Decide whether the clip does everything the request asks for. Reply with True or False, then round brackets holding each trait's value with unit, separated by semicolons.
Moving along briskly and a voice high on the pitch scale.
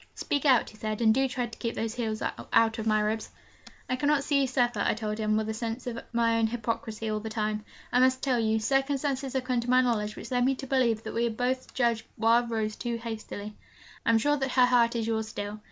True (250 wpm; 230 Hz)